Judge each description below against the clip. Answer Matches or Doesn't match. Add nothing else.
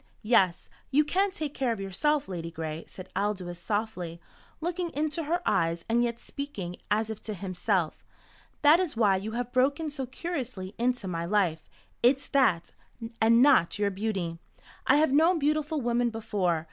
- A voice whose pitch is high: Matches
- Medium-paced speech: Matches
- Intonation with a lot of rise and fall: Matches